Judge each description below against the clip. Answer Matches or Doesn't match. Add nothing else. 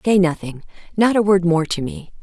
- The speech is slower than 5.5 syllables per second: Matches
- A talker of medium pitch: Matches